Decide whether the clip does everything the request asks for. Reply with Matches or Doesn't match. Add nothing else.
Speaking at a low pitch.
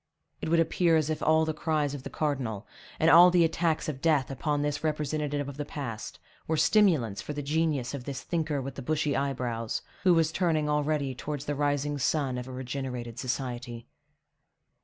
Doesn't match